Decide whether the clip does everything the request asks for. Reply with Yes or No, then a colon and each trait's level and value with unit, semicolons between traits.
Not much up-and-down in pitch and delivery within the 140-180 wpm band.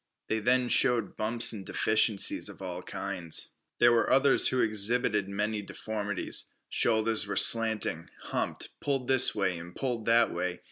No: average, 3.3 semitones; average, 150 wpm